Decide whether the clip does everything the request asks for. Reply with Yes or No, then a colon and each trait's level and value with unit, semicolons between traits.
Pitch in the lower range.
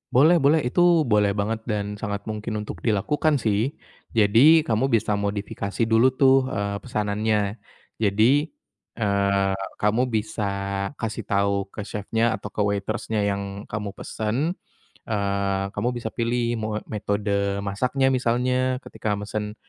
Yes: low, 105 Hz